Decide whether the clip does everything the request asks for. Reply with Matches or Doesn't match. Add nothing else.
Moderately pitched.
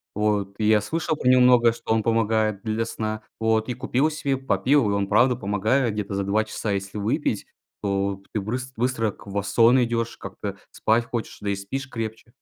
Doesn't match